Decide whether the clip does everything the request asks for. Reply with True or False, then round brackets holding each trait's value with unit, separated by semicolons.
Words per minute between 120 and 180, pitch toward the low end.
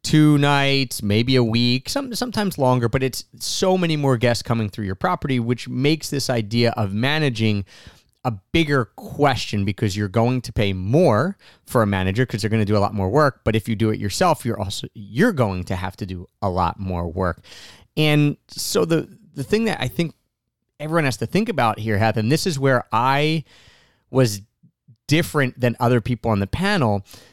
False (200 wpm; 120 Hz)